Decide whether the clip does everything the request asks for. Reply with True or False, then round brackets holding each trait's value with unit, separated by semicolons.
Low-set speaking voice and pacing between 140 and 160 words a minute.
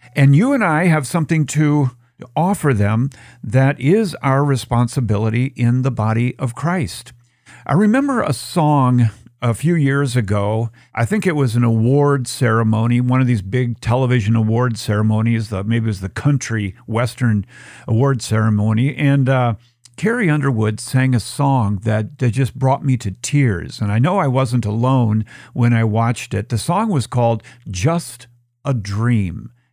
True (125 Hz; 155 wpm)